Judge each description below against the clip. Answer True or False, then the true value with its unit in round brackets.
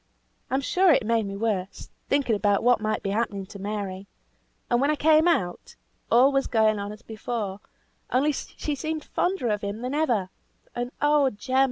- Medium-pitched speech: False (230 Hz)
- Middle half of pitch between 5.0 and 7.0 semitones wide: True (5.5 semitones)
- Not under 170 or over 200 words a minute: True (185 wpm)